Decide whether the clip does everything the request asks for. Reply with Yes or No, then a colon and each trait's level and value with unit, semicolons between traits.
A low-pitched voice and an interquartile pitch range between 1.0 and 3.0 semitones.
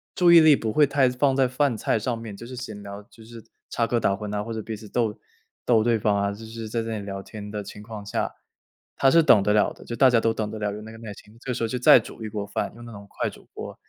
Yes: low, 110 Hz; narrow, 2.6 semitones